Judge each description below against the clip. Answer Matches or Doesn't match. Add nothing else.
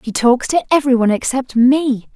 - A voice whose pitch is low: Doesn't match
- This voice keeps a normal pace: Matches